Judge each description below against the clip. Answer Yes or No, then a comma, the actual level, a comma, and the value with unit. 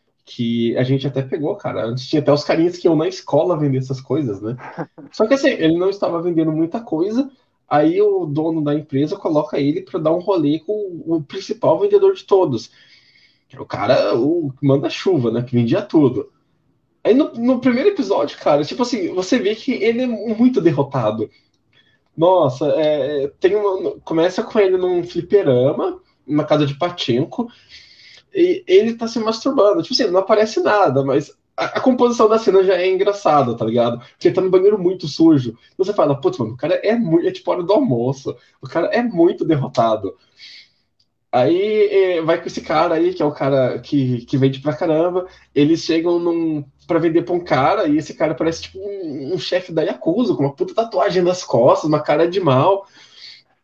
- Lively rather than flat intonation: Yes, wide, 8.7 semitones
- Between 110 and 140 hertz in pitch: No, medium, 180 Hz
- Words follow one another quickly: Yes, fast, 190 wpm